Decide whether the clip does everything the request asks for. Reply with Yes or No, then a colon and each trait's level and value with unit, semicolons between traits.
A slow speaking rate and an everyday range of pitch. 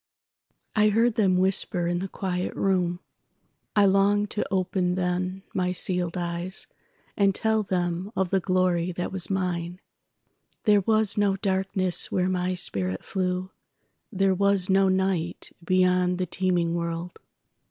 No: slow, 125 wpm; narrow, 1.6 semitones